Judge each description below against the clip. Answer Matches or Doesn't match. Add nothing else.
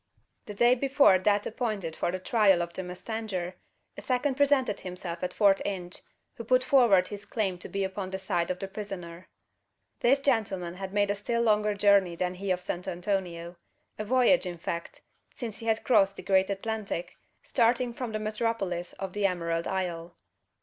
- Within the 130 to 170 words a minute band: Doesn't match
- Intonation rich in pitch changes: Doesn't match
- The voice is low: Doesn't match